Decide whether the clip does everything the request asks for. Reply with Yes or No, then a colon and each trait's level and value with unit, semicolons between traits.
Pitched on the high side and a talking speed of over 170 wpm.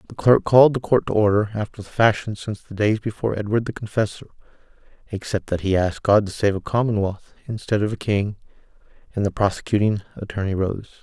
No: low, 105 Hz; average, 180 wpm